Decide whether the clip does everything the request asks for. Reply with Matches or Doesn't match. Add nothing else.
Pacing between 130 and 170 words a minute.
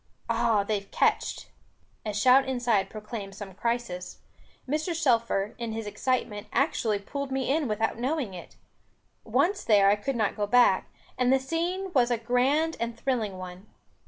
Matches